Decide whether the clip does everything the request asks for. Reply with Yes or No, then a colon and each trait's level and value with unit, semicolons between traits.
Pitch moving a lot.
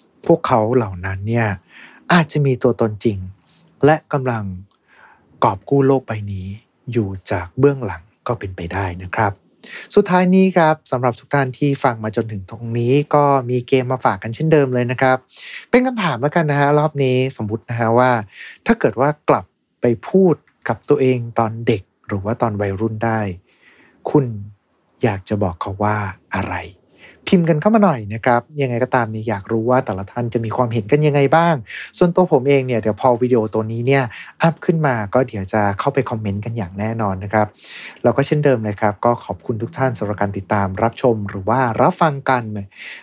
No: average, 4.4 semitones